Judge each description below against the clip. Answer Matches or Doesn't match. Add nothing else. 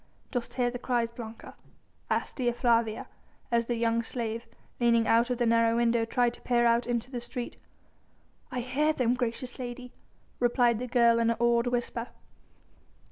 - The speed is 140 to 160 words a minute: Doesn't match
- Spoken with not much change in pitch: Matches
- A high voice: Matches